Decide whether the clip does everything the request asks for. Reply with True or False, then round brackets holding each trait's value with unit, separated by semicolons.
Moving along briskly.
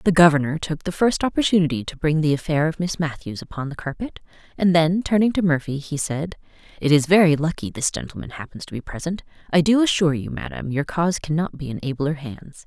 True (215 wpm)